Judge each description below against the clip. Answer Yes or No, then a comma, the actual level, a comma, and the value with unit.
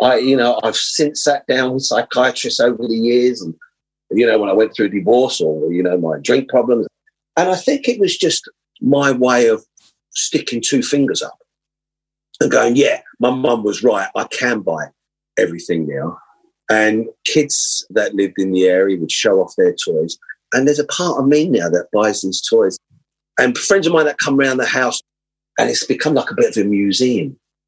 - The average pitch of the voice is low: Yes, low, 130 Hz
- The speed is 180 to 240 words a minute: Yes, average, 200 wpm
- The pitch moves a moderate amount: No, wide, 6.0 semitones